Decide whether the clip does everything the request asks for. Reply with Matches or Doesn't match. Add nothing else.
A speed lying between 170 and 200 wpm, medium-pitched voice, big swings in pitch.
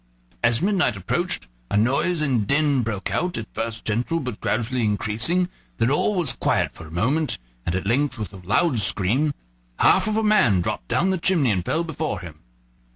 Doesn't match